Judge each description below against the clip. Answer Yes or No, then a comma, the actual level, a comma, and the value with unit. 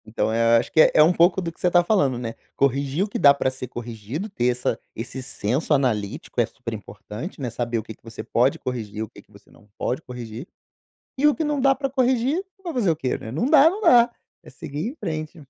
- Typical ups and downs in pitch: No, wide, 9.0 semitones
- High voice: No, medium, 140 Hz